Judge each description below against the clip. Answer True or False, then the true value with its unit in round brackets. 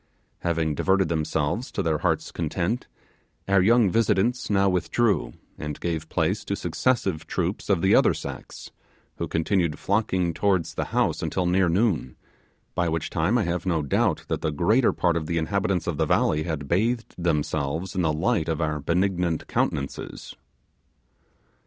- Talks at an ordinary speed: True (160 wpm)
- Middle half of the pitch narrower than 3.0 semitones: False (3.6 semitones)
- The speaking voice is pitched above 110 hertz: False (85 Hz)